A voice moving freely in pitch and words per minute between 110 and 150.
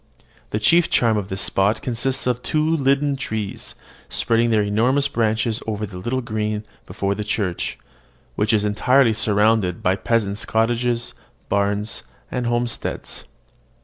No: average, 2.9 semitones; average, 140 wpm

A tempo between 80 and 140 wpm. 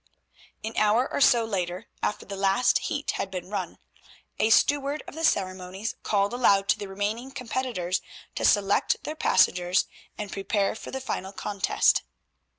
No: average, 155 wpm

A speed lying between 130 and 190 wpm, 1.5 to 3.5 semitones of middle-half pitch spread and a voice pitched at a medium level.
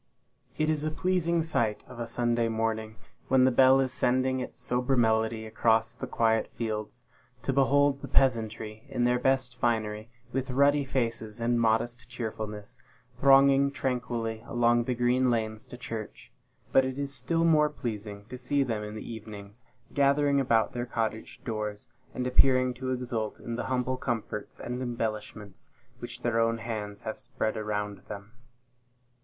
No: average, 160 wpm; average, 2.9 semitones; low, 120 Hz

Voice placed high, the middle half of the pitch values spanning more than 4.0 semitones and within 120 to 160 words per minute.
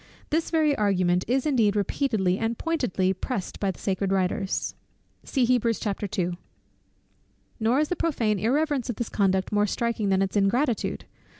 Yes: high, 215 Hz; average, 5.3 semitones; slow, 135 wpm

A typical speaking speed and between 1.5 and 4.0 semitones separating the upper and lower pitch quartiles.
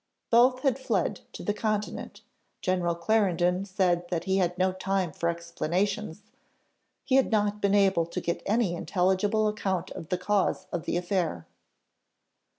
Yes: average, 155 wpm; average, 3.0 semitones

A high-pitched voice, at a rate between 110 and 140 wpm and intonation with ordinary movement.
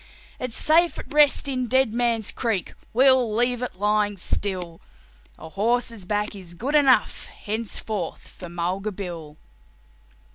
Yes: high, 215 Hz; slow, 135 wpm; average, 4.8 semitones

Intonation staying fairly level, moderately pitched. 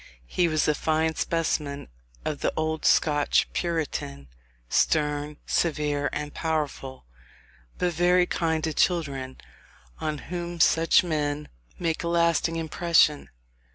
Yes: narrow, 2.3 semitones; medium, 155 Hz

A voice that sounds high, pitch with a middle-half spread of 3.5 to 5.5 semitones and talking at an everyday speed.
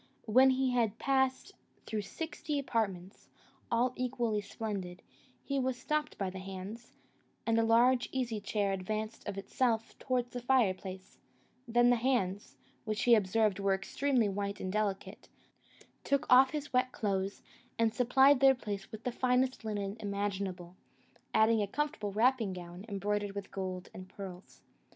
Yes: high, 220 Hz; average, 4.2 semitones; average, 150 wpm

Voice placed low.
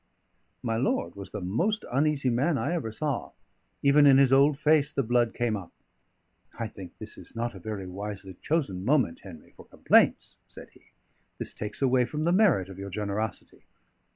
Yes: low, 120 Hz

